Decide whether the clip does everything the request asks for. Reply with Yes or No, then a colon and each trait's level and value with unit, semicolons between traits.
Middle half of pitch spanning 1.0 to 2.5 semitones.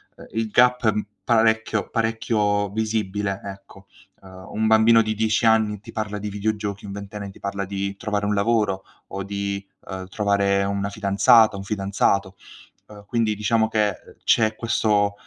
Yes: narrow, 1.8 semitones